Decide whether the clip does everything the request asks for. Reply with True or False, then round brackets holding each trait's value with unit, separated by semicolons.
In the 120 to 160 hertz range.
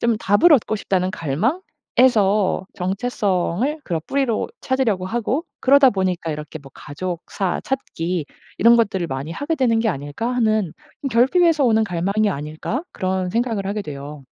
False (205 Hz)